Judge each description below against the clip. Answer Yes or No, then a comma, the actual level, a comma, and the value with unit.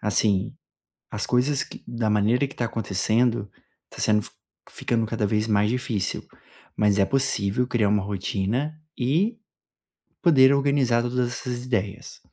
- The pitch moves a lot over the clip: No, average, 3.4 semitones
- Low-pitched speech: Yes, low, 115 Hz